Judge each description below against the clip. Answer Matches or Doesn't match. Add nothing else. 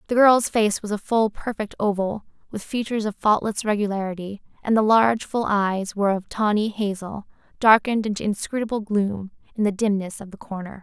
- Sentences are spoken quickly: Doesn't match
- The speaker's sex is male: Doesn't match